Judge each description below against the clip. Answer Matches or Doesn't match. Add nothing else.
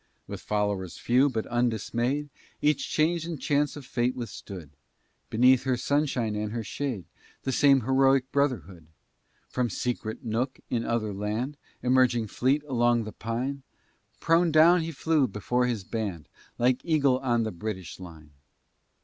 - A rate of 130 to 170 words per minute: Matches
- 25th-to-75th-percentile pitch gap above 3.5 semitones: Matches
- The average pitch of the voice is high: Doesn't match